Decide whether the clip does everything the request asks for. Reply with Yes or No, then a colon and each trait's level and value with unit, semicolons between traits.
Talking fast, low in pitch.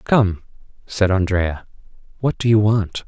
No: slow, 135 wpm; low, 100 Hz